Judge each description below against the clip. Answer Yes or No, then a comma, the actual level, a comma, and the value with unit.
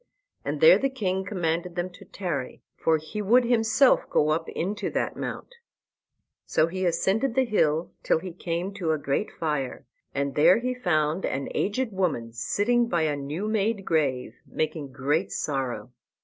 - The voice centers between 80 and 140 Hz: No, medium, 175 Hz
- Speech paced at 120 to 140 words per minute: No, average, 165 wpm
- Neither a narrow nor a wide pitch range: No, wide, 5.7 semitones